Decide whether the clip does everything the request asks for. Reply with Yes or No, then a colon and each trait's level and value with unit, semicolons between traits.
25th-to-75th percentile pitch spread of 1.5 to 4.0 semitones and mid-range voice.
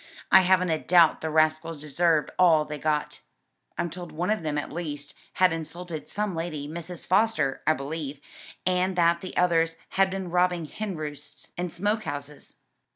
Yes: average, 2.9 semitones; medium, 165 Hz